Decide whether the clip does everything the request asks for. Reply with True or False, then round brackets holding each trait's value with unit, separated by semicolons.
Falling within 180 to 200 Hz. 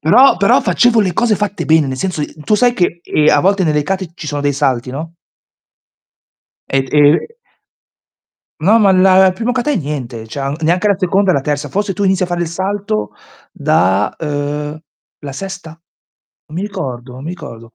False (165 Hz)